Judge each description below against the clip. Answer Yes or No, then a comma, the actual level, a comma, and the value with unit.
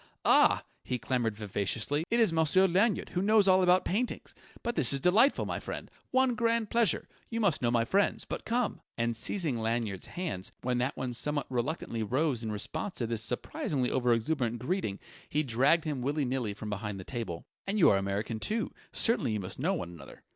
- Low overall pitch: Yes, low, 130 Hz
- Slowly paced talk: No, average, 195 wpm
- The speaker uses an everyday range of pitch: No, wide, 8.6 semitones